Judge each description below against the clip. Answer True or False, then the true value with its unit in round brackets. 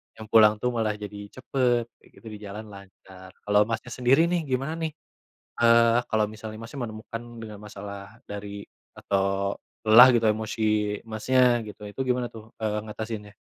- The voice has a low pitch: True (110 Hz)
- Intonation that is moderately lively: False (2.3 semitones)